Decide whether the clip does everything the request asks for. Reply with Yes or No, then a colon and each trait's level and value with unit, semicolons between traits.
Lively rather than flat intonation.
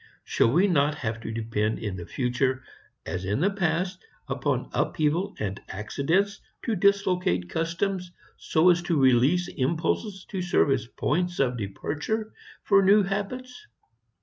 Yes: wide, 7.7 semitones